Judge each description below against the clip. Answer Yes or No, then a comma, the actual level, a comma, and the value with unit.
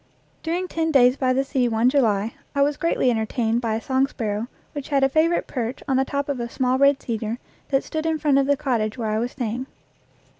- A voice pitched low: No, very high, 260 Hz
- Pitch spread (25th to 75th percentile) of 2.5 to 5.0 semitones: Yes, average, 3.4 semitones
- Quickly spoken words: Yes, fast, 230 wpm